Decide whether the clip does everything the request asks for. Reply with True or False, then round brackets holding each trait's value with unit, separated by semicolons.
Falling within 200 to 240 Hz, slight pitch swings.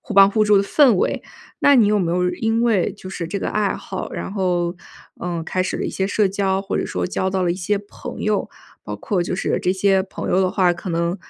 False (190 Hz; 2.2 semitones)